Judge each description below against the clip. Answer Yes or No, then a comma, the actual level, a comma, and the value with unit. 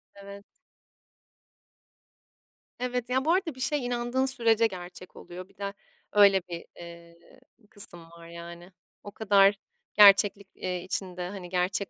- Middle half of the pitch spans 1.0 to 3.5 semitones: No, average, 4.4 semitones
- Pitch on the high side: Yes, high, 200 Hz